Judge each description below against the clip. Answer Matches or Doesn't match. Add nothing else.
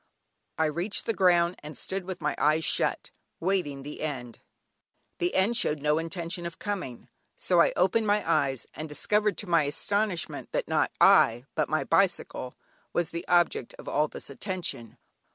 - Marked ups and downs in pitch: Doesn't match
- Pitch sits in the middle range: Matches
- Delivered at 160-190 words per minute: Matches